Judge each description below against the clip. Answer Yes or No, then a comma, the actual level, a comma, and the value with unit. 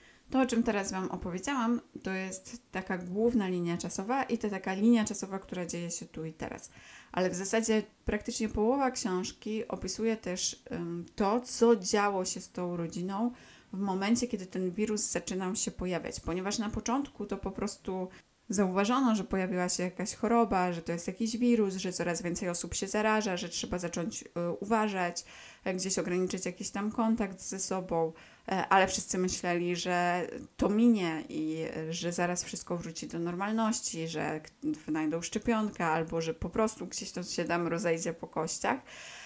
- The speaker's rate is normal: No, fast, 165 wpm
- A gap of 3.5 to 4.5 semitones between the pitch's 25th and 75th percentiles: Yes, average, 3.8 semitones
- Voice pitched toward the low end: No, high, 190 Hz